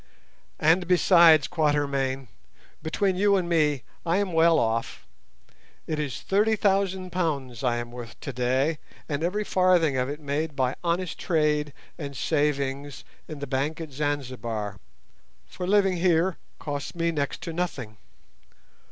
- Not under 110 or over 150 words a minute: Yes, average, 140 wpm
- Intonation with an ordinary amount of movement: Yes, average, 4.4 semitones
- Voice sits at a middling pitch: Yes, medium, 150 Hz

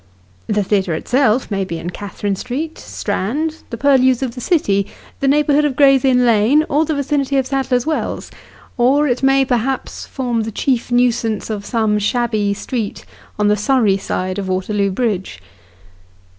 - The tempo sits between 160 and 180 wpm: Yes, average, 170 wpm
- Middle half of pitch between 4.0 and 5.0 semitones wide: Yes, average, 4.7 semitones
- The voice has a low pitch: No, high, 240 Hz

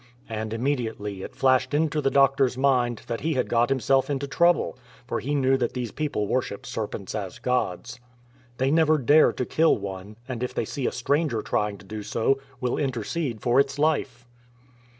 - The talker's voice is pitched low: Yes, low, 125 Hz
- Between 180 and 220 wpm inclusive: Yes, average, 190 wpm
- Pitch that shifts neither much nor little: Yes, average, 3.7 semitones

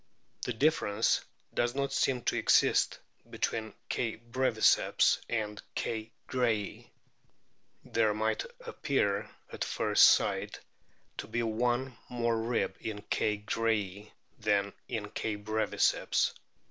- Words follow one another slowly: Yes, slow, 110 wpm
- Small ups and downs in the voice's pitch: Yes, narrow, 2.3 semitones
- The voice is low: Yes, low, 110 Hz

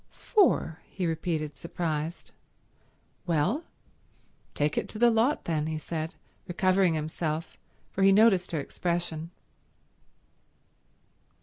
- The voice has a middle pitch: Yes, medium, 170 Hz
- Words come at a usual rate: No, slow, 105 wpm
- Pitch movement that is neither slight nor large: Yes, average, 3.6 semitones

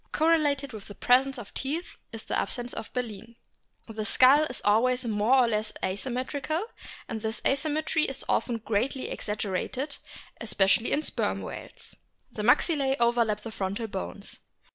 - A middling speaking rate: Yes, average, 150 wpm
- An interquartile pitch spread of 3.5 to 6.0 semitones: Yes, average, 4.0 semitones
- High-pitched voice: Yes, high, 240 Hz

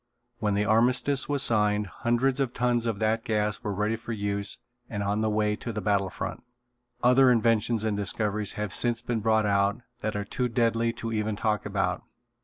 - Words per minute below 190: No, average, 195 wpm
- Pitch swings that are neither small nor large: No, narrow, 2.1 semitones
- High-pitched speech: No, low, 110 Hz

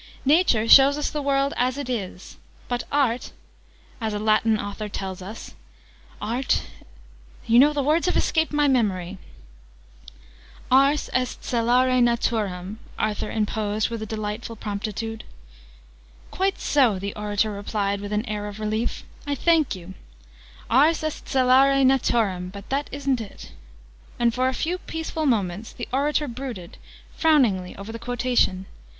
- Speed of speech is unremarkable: Yes, average, 145 wpm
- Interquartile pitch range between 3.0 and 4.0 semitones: No, average, 4.8 semitones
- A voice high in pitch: Yes, high, 230 Hz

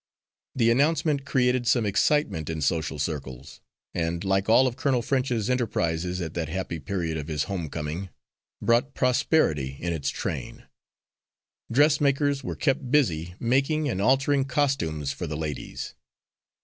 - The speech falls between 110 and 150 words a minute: Yes, average, 140 wpm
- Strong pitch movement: Yes, wide, 8.9 semitones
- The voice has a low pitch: Yes, low, 105 Hz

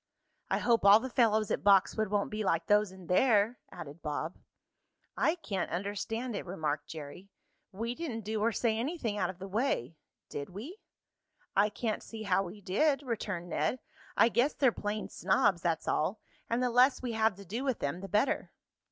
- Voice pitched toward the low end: No, high, 210 Hz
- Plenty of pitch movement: No, average, 4.1 semitones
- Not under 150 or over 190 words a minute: Yes, average, 185 wpm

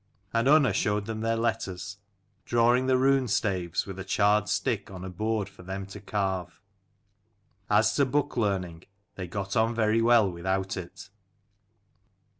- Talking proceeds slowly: No, average, 150 wpm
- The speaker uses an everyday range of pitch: Yes, average, 3.3 semitones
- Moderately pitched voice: No, low, 105 Hz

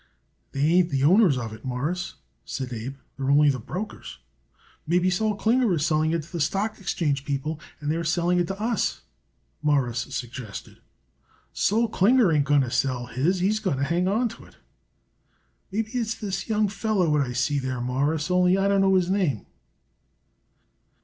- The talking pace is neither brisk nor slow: Yes, average, 175 wpm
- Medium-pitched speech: Yes, medium, 165 Hz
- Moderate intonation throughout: No, wide, 6.0 semitones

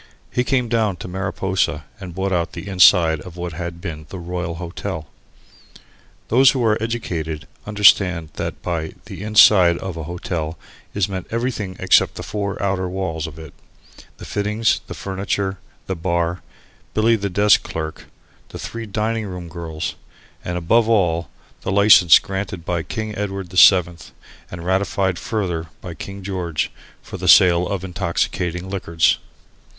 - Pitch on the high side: No, very low, 95 Hz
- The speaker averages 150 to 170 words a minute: Yes, average, 155 wpm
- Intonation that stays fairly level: No, average, 3.1 semitones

